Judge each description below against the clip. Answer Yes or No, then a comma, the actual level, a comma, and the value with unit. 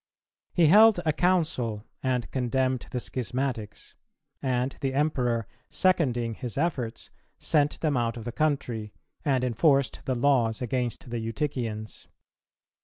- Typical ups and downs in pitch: Yes, average, 3.8 semitones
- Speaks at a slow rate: Yes, slow, 125 wpm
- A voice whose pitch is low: Yes, low, 130 Hz